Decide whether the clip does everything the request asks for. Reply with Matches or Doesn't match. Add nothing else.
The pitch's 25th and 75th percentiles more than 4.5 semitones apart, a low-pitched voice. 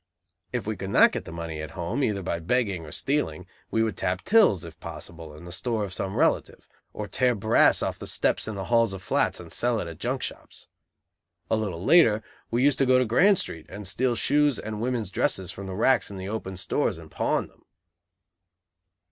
Matches